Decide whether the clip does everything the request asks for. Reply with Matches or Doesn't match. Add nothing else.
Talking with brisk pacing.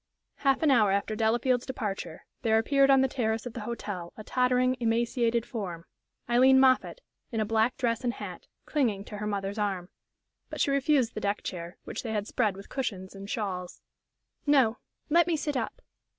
Doesn't match